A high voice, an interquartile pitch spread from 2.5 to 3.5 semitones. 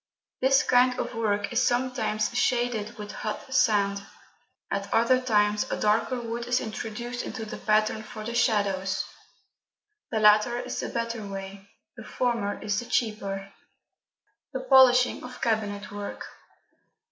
Yes: high, 220 Hz; average, 2.9 semitones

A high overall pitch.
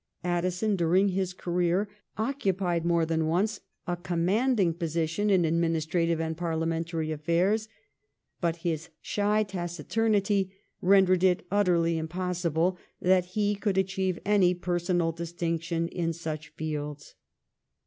No: medium, 175 Hz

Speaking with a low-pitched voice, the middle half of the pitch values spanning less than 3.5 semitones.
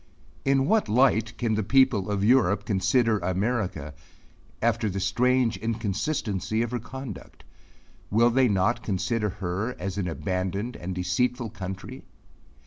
No: low, 110 Hz; average, 4.2 semitones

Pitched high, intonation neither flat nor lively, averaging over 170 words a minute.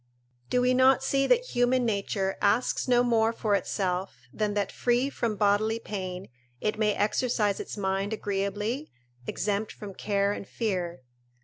No: high, 210 Hz; average, 3.5 semitones; average, 150 wpm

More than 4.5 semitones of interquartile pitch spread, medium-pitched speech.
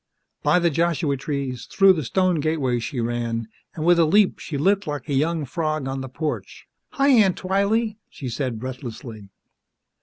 Yes: wide, 5.6 semitones; medium, 155 Hz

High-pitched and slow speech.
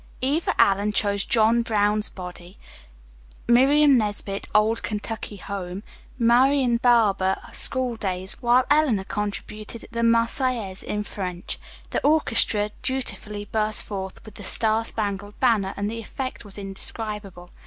Yes: high, 215 Hz; slow, 120 wpm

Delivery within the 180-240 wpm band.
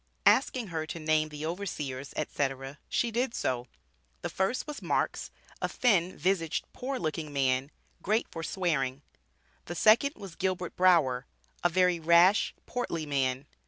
No: average, 145 wpm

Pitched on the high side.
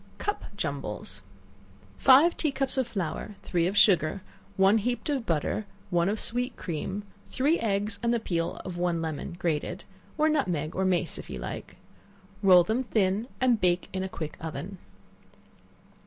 Yes: high, 195 Hz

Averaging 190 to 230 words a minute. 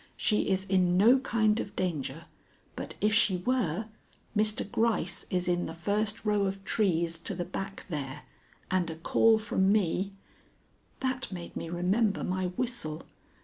No: average, 160 wpm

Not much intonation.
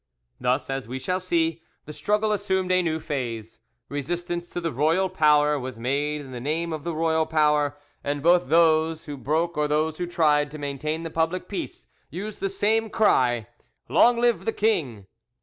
No: average, 3.3 semitones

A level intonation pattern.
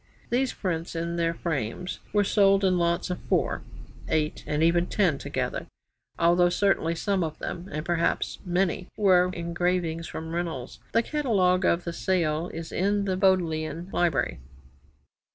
Yes: narrow, 2.3 semitones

